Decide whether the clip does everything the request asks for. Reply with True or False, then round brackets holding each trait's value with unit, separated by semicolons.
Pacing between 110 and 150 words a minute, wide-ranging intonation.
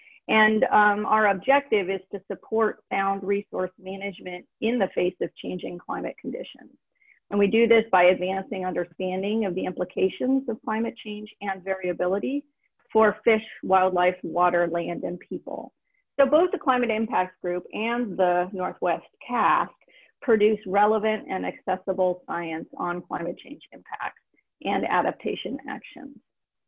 False (135 wpm; 3.2 semitones)